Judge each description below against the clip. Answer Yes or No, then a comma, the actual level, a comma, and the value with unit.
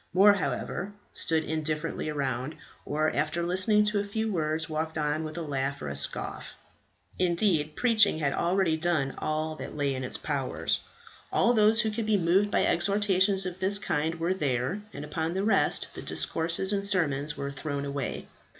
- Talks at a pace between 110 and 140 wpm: No, average, 175 wpm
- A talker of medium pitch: Yes, medium, 165 Hz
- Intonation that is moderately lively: Yes, average, 4.8 semitones